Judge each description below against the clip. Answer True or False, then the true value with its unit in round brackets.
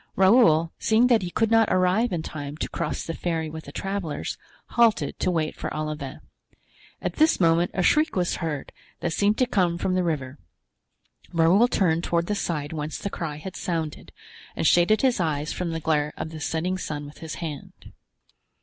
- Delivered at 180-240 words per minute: True (190 wpm)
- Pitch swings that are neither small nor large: True (3.7 semitones)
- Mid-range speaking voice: True (170 Hz)